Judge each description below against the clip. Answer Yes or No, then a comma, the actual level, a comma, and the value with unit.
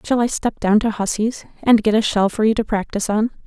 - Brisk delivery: Yes, fast, 260 wpm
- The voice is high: Yes, high, 215 Hz